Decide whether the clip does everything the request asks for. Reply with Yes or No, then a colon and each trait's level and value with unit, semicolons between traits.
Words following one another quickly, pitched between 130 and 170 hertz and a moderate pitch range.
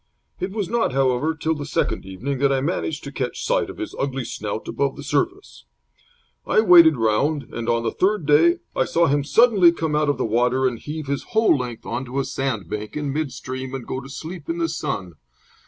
Yes: fast, 220 wpm; medium, 140 Hz; average, 4.3 semitones